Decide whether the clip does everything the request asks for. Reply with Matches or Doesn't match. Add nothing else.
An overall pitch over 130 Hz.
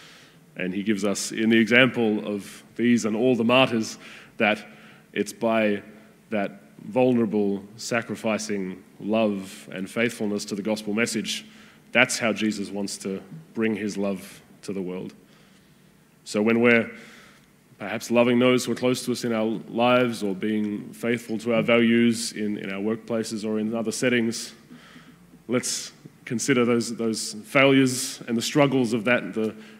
Doesn't match